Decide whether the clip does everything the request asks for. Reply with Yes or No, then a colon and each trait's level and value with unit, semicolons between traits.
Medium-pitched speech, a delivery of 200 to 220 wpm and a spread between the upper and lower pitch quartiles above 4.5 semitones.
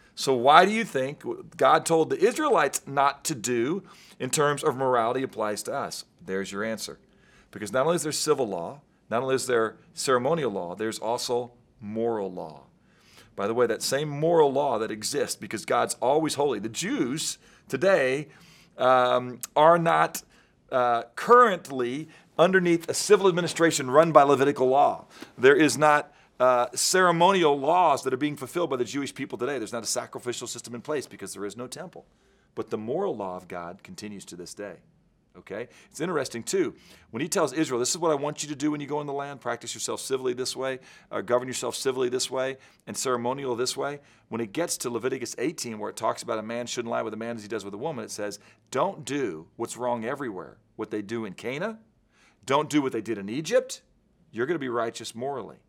No: low, 130 Hz; fast, 205 wpm; average, 5.0 semitones